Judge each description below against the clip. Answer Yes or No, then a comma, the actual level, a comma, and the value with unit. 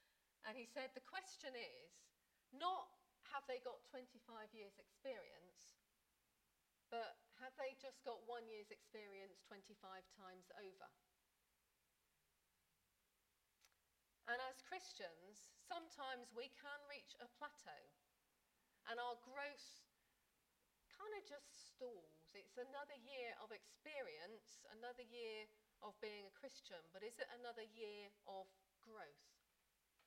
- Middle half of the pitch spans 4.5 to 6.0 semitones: Yes, average, 5.0 semitones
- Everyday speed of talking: No, slow, 115 wpm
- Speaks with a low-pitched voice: No, high, 245 Hz